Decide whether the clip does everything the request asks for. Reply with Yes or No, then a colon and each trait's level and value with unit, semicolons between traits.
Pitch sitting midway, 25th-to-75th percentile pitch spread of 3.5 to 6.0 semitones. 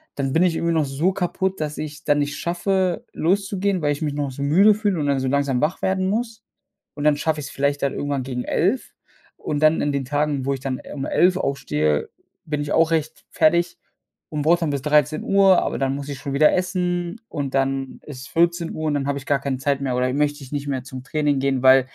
Yes: medium, 145 Hz; average, 3.8 semitones